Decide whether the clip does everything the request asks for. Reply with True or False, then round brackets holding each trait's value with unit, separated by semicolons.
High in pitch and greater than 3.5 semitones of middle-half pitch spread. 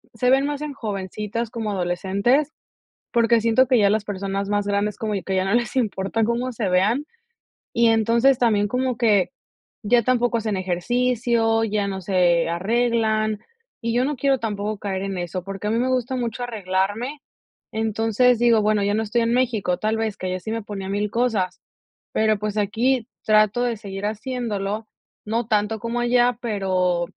False (220 Hz; 3.1 semitones)